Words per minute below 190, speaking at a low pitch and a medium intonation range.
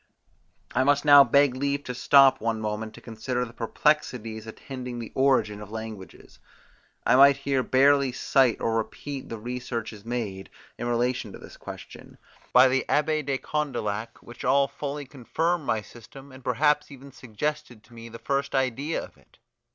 Yes: average, 165 wpm; low, 130 Hz; average, 3.5 semitones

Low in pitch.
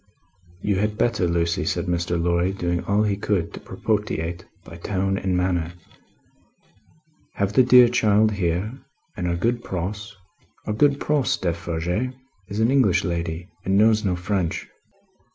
Yes: very low, 95 Hz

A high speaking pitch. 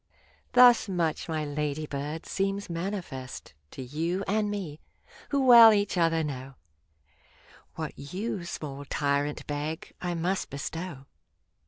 No: medium, 165 Hz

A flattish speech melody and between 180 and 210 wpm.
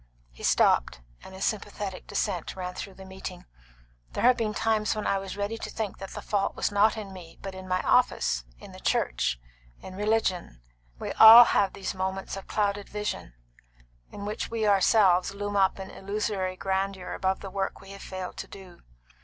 Yes: narrow, 1.8 semitones; average, 190 wpm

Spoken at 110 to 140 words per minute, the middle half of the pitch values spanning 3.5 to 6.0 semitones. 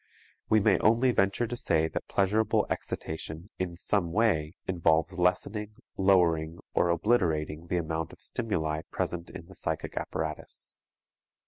Yes: slow, 135 wpm; average, 4.5 semitones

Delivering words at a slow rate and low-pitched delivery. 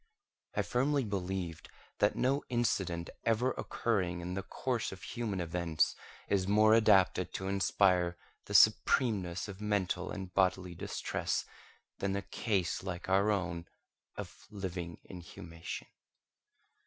Yes: slow, 125 wpm; very low, 95 Hz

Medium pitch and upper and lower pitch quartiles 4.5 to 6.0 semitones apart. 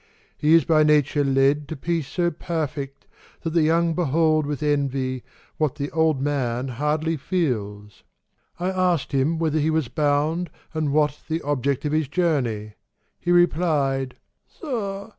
No: medium, 150 Hz; average, 3.1 semitones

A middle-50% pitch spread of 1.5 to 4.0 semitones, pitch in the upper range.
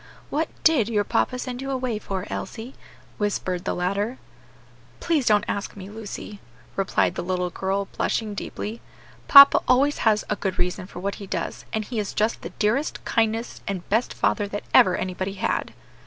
Yes: average, 3.4 semitones; high, 210 Hz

